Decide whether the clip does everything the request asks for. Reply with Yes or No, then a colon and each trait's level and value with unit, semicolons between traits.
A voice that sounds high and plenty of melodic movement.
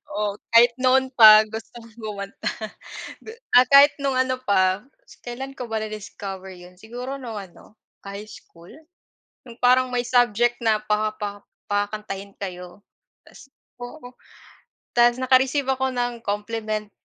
No: high, 225 Hz; average, 3.5 semitones